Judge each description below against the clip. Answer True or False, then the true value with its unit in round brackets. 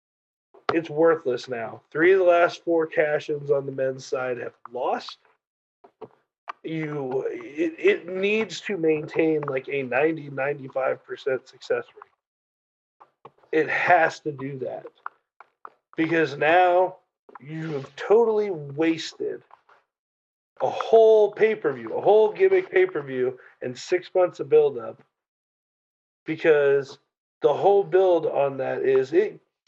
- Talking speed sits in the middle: False (120 wpm)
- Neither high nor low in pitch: True (180 Hz)